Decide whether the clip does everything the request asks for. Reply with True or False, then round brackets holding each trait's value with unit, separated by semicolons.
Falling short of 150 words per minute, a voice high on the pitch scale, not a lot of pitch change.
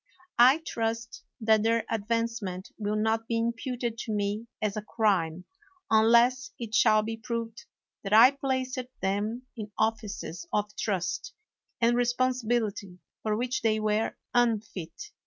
True (140 wpm; 225 Hz; 2.1 semitones)